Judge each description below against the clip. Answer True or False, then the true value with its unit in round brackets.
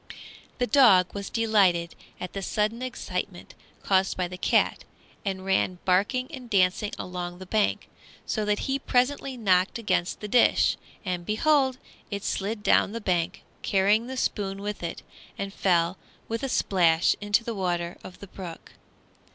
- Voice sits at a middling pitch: False (200 Hz)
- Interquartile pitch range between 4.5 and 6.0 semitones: False (3.9 semitones)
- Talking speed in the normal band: True (160 wpm)